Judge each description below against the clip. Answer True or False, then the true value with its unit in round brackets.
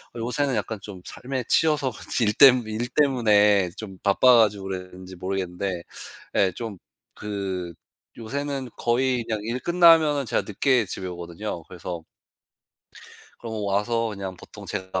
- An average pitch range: True (4.9 semitones)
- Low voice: True (110 Hz)